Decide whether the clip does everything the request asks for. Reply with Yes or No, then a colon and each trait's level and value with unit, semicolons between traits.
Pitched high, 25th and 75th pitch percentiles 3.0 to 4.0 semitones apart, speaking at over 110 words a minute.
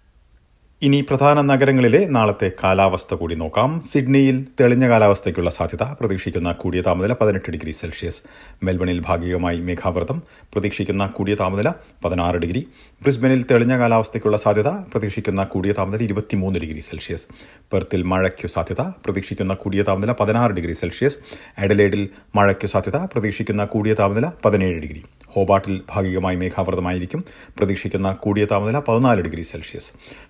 No: low, 100 Hz; average, 3.7 semitones; average, 120 wpm